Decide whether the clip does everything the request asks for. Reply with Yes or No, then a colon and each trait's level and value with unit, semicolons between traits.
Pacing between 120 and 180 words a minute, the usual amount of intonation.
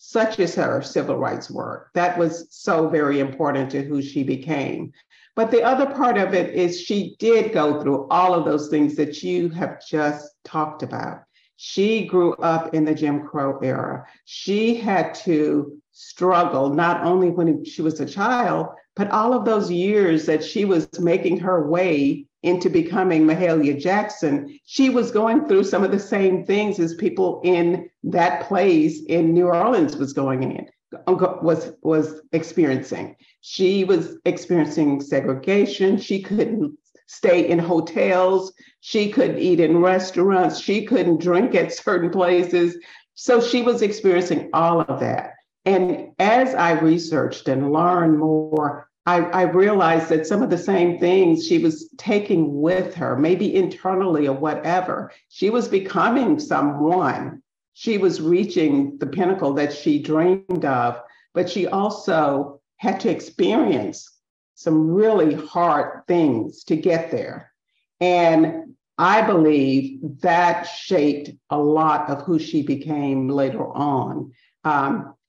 Yes: average, 145 wpm; average, 3.8 semitones